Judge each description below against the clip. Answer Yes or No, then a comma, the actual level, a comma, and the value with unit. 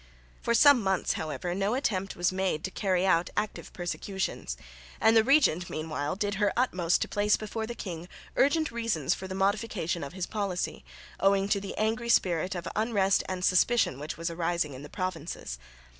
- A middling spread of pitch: Yes, average, 3.7 semitones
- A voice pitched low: No, high, 190 Hz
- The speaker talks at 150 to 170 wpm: No, average, 180 wpm